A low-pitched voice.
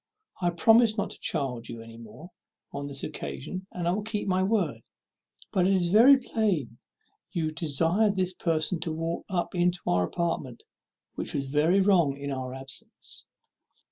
No: medium, 170 Hz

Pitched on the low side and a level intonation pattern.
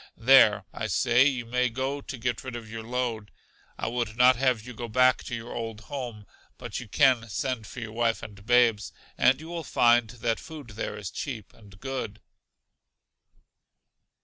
Yes: low, 120 Hz; narrow, 2.3 semitones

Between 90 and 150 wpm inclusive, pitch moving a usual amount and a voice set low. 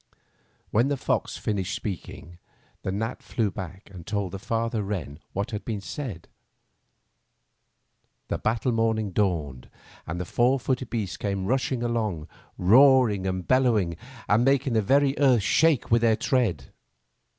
Yes: average, 145 wpm; average, 4.7 semitones; low, 110 Hz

